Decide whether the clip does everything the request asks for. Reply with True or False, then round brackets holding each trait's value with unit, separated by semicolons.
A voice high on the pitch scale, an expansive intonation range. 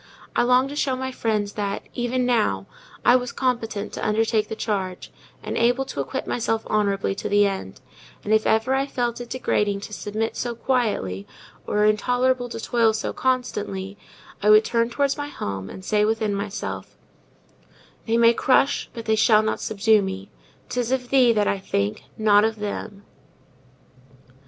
False (220 Hz; 3.2 semitones)